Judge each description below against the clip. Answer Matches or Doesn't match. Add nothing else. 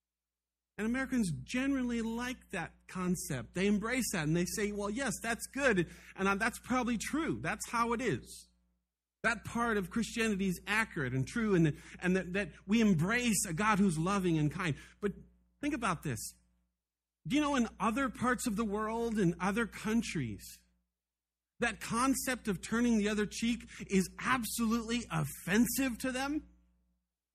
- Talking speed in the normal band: Matches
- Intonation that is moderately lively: Doesn't match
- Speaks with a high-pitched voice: Matches